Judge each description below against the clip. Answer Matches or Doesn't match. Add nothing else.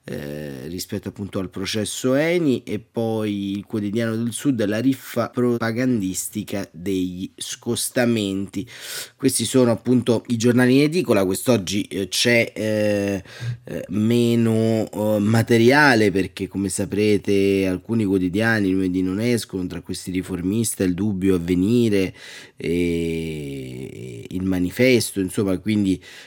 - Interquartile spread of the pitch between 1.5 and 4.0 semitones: Matches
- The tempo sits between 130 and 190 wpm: Doesn't match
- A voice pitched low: Matches